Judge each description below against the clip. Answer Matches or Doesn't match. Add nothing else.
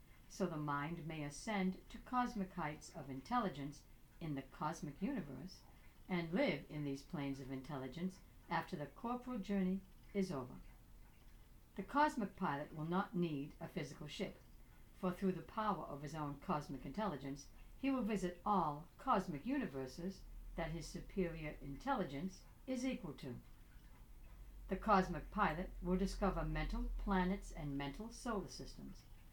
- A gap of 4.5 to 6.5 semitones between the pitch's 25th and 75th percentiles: Matches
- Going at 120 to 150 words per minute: Matches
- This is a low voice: Doesn't match